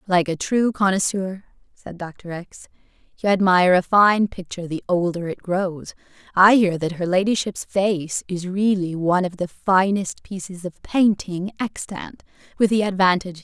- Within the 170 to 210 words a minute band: No, average, 160 wpm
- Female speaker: Yes, female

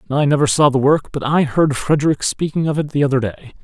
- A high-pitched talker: No, medium, 145 Hz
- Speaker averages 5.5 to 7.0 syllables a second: Yes, 6.0 syllables/s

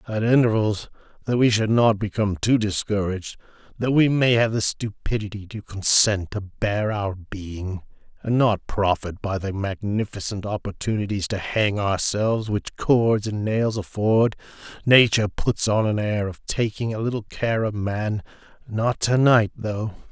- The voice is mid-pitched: No, low, 105 Hz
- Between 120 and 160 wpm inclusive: Yes, average, 150 wpm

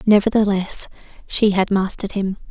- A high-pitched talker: Yes, high, 200 Hz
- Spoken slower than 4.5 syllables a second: No, 5.3 syllables/s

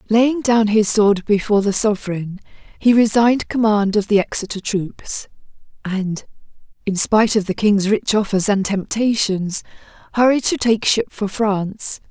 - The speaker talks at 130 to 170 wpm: Yes, average, 150 wpm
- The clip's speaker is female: Yes, female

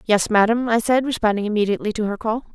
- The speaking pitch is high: Yes, high, 220 Hz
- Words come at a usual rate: No, fast, 210 wpm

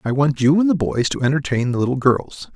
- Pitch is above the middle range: No, low, 135 Hz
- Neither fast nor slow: No, fast, 260 wpm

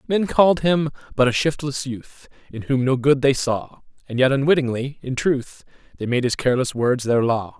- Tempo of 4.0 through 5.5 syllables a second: Yes, 5.1 syllables/s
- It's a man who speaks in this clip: Yes, male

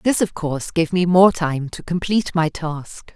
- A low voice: No, medium, 170 Hz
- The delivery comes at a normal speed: No, fast, 210 wpm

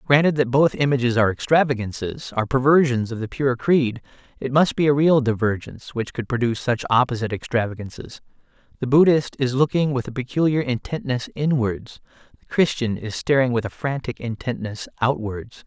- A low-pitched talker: Yes, low, 125 Hz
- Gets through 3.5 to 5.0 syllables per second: No, 5.6 syllables/s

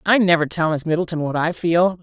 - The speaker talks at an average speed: No, fast, 235 wpm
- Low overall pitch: No, medium, 170 Hz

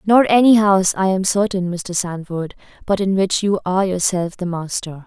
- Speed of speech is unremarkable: Yes, average, 190 wpm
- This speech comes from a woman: Yes, female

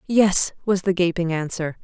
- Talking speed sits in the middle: Yes, average, 165 wpm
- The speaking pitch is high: No, medium, 180 Hz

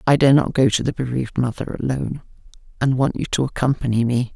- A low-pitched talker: Yes, low, 130 Hz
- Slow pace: No, fast, 205 wpm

